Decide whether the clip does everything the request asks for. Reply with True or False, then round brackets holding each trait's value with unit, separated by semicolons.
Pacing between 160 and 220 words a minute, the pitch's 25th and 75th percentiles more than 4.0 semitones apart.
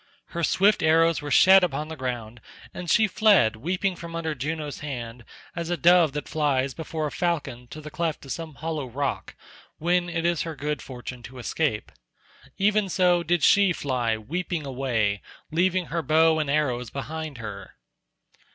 True (170 wpm; 4.6 semitones)